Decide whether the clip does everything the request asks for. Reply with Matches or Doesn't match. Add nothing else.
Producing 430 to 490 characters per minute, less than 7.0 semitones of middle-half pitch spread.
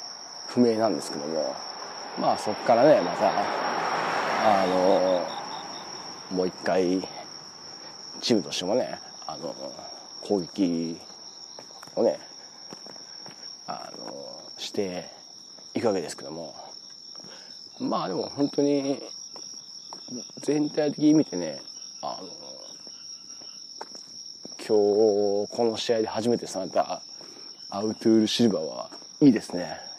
Doesn't match